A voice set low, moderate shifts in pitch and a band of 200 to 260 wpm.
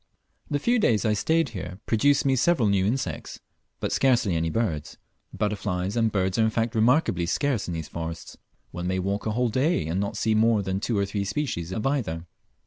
Yes: low, 105 Hz; average, 4.8 semitones; fast, 205 wpm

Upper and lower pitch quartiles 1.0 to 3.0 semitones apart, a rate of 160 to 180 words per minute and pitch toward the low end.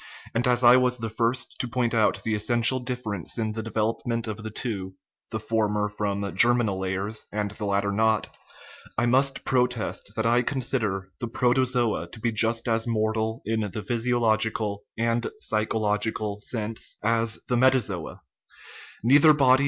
Yes: narrow, 2.4 semitones; average, 165 wpm; low, 115 Hz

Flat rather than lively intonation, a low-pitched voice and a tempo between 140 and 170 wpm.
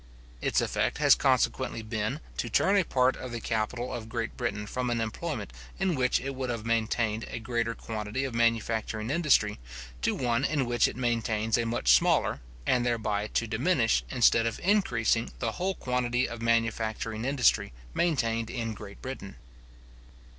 Yes: narrow, 2.2 semitones; low, 115 Hz; average, 165 wpm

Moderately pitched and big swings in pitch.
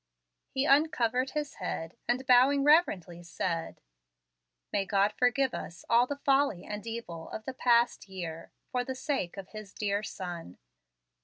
No: high, 230 Hz; wide, 5.9 semitones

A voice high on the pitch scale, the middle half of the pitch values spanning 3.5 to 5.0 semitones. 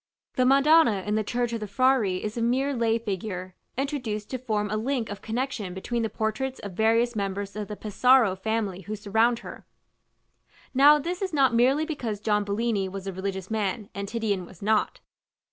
Yes: high, 220 Hz; average, 3.8 semitones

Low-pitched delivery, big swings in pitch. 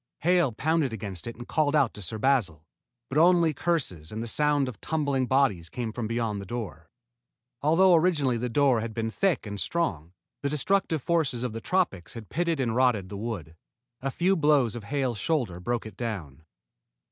Yes: low, 125 Hz; wide, 6.0 semitones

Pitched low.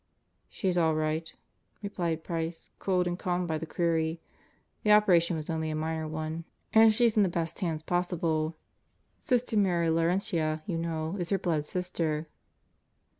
No: medium, 165 Hz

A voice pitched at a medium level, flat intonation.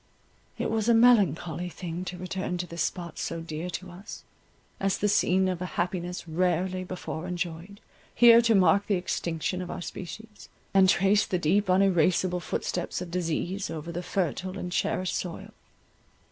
Yes: medium, 180 Hz; narrow, 2.0 semitones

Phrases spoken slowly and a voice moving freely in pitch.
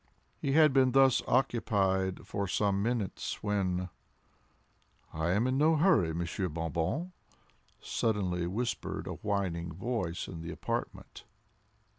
Yes: slow, 125 wpm; wide, 5.9 semitones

